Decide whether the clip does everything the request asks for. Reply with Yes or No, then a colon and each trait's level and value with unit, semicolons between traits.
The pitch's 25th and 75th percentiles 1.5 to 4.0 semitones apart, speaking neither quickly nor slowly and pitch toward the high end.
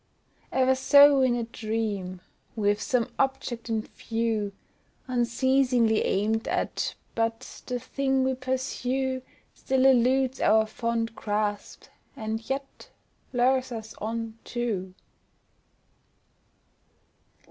No: average, 2.9 semitones; slow, 100 wpm; high, 235 Hz